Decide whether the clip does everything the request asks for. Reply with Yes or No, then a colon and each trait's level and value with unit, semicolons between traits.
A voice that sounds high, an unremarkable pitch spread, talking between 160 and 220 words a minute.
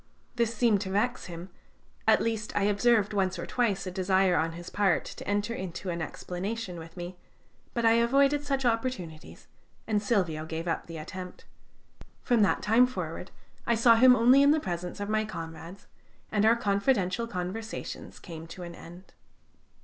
Yes: high, 205 Hz; average, 4.6 semitones; average, 170 wpm